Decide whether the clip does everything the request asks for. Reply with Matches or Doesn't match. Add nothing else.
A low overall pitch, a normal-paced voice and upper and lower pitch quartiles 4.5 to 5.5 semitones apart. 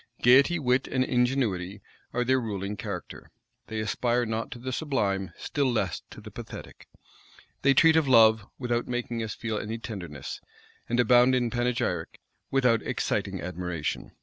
Doesn't match